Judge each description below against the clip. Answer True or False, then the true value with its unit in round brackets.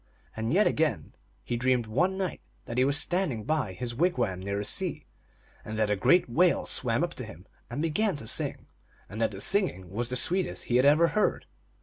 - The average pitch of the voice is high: False (125 Hz)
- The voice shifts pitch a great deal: True (7.7 semitones)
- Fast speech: True (210 wpm)